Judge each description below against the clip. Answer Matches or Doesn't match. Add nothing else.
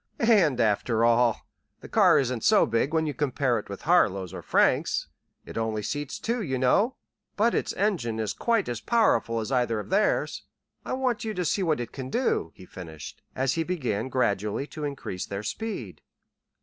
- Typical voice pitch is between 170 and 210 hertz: Doesn't match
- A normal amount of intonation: Doesn't match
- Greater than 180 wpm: Matches